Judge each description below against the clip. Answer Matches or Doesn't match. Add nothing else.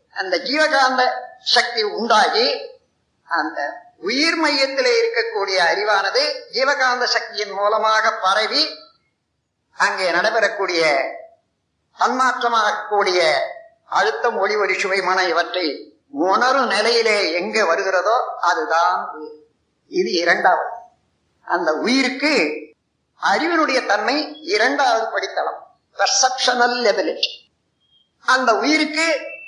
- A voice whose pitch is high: Matches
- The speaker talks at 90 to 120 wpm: Doesn't match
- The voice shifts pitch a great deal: Matches